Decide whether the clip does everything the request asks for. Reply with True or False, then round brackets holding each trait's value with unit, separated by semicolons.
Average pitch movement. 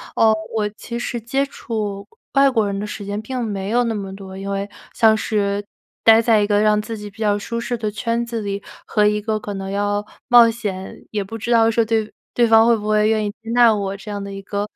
False (2.0 semitones)